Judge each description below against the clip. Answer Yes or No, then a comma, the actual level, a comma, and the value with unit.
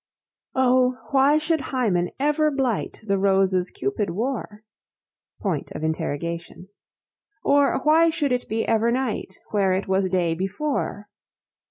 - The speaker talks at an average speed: No, slow, 110 wpm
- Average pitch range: No, wide, 6.6 semitones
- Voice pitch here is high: Yes, high, 210 Hz